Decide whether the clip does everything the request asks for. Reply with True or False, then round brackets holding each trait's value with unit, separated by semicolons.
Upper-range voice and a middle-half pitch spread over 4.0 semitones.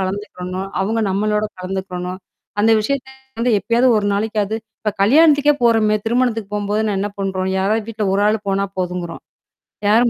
False (210 Hz; 2.7 semitones)